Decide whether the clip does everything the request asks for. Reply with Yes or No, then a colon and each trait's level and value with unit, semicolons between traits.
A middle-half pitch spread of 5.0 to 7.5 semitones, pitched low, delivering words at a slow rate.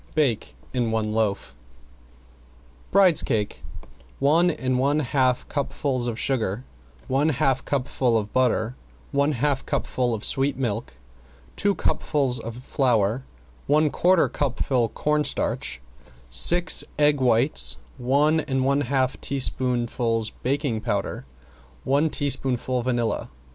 No: average, 3.2 semitones; low, 130 Hz; slow, 115 wpm